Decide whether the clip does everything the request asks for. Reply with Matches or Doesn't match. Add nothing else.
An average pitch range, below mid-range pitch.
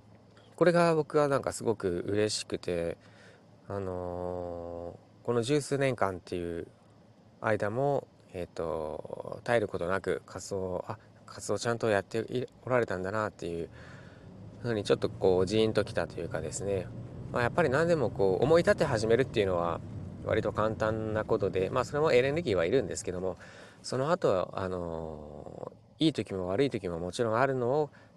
Doesn't match